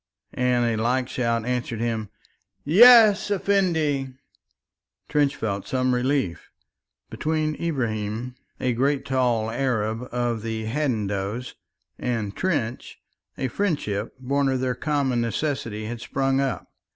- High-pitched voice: No, low, 125 Hz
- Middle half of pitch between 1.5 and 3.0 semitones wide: No, average, 3.8 semitones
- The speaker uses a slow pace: Yes, slow, 115 wpm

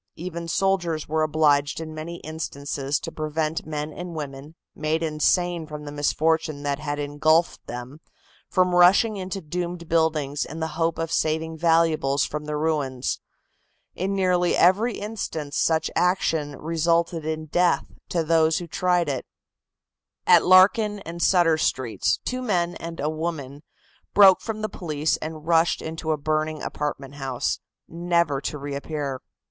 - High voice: No, medium, 160 Hz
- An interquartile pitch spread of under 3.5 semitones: Yes, narrow, 2.4 semitones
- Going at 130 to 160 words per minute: Yes, average, 150 wpm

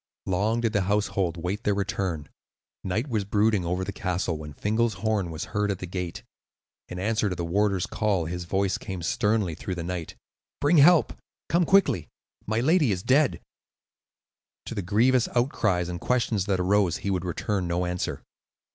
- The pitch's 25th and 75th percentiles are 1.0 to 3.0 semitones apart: No, average, 3.5 semitones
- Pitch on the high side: No, low, 100 Hz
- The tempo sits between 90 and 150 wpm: No, average, 180 wpm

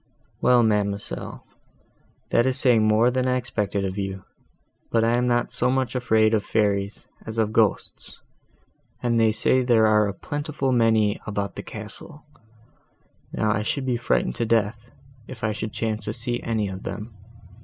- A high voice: No, low, 110 Hz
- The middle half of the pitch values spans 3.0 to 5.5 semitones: No, narrow, 2.6 semitones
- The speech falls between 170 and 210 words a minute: Yes, average, 175 wpm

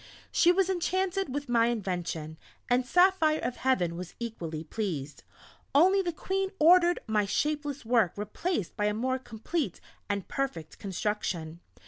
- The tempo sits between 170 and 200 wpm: No, average, 140 wpm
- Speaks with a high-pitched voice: Yes, high, 240 Hz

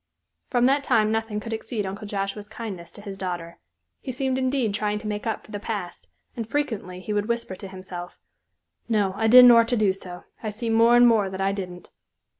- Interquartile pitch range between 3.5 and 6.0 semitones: No, average, 3.1 semitones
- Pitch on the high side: Yes, high, 210 Hz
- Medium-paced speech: No, fast, 210 wpm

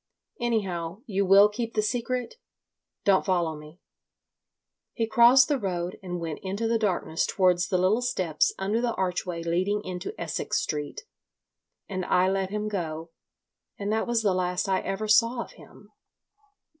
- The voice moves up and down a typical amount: Yes, average, 3.8 semitones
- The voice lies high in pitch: Yes, high, 195 Hz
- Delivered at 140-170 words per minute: Yes, average, 155 wpm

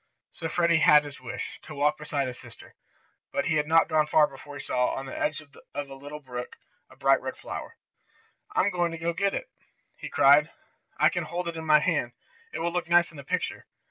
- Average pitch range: Yes, average, 3.0 semitones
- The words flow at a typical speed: No, fast, 220 wpm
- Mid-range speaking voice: Yes, medium, 150 Hz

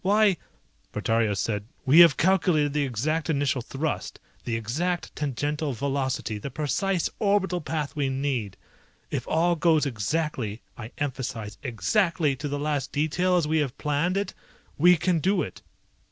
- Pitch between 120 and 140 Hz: No, medium, 150 Hz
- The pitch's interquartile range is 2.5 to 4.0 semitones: No, average, 4.4 semitones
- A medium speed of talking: Yes, average, 155 wpm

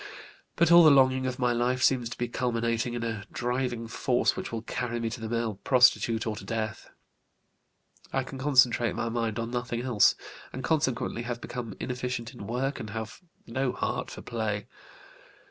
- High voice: No, low, 120 Hz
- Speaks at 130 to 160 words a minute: No, average, 180 wpm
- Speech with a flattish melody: Yes, narrow, 1.9 semitones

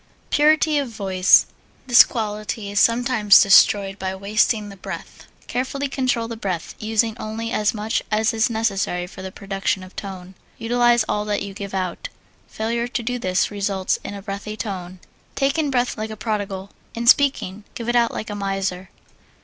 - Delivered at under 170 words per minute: No, average, 175 wpm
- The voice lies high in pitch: Yes, high, 215 Hz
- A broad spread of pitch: No, average, 3.2 semitones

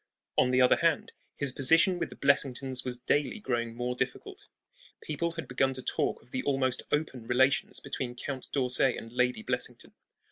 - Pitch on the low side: Yes, low, 130 Hz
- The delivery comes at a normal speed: Yes, average, 175 wpm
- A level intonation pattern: Yes, narrow, 2.3 semitones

